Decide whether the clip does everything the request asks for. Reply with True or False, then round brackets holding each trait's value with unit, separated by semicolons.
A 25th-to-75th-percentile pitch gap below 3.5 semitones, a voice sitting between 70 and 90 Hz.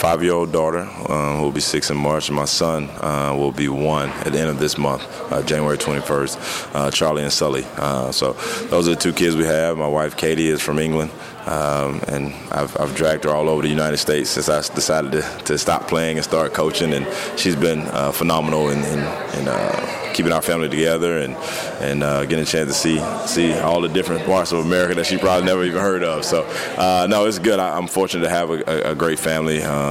True (2.4 semitones; 80 Hz)